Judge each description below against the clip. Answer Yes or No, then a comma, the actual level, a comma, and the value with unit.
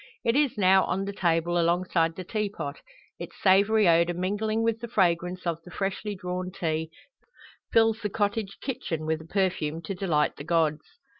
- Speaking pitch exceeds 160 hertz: Yes, medium, 185 Hz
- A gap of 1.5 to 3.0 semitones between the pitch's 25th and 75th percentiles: No, average, 3.7 semitones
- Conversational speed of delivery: Yes, average, 170 wpm